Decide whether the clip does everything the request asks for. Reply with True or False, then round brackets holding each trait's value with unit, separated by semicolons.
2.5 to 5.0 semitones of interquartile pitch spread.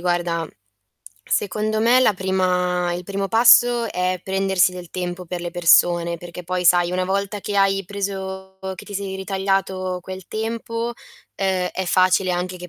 False (1.7 semitones)